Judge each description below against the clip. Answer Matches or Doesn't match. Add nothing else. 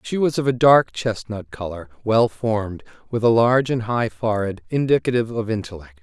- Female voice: Doesn't match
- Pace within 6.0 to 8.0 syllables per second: Doesn't match